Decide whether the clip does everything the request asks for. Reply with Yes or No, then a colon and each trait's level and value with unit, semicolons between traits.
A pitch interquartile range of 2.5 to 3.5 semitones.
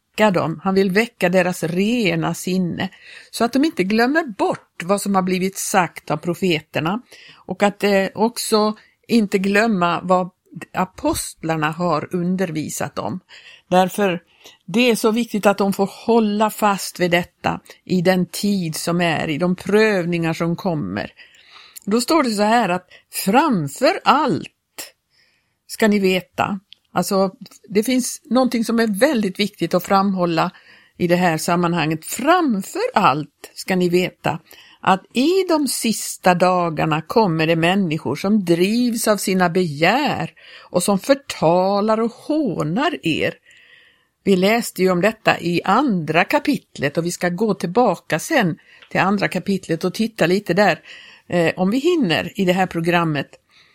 No: average, 4.3 semitones